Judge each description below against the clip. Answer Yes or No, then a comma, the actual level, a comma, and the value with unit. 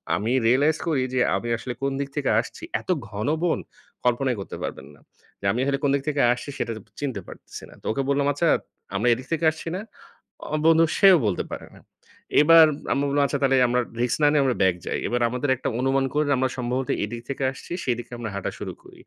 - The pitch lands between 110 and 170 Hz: Yes, low, 135 Hz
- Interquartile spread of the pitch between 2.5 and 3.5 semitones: Yes, average, 3.0 semitones